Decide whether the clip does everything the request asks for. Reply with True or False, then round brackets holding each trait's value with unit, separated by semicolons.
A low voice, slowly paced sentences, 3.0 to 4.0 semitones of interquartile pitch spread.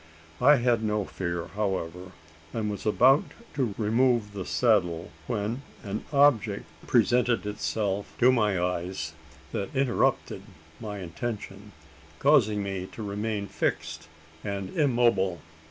True (105 Hz; 120 wpm; 3.7 semitones)